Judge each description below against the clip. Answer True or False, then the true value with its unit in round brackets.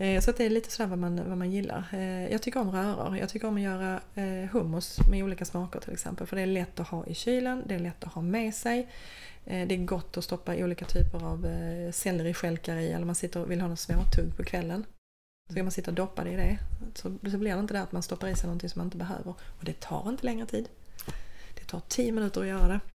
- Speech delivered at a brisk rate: True (260 wpm)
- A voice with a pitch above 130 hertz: True (185 Hz)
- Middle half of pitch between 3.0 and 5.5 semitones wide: False (2.5 semitones)